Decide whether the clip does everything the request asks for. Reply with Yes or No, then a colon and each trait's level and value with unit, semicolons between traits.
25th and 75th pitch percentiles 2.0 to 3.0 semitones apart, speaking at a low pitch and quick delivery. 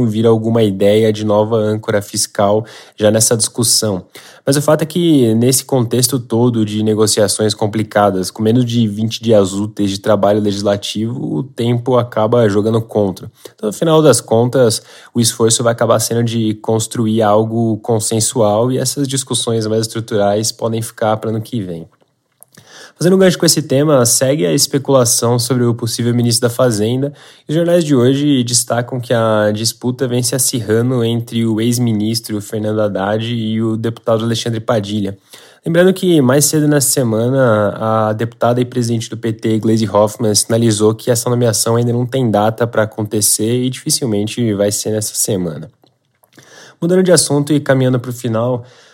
No: narrow, 2.6 semitones; low, 115 Hz; average, 165 wpm